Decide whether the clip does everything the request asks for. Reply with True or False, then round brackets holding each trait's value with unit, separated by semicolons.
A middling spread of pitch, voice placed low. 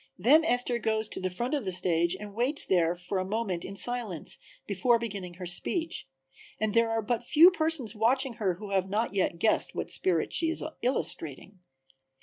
False (4.9 semitones; 215 Hz)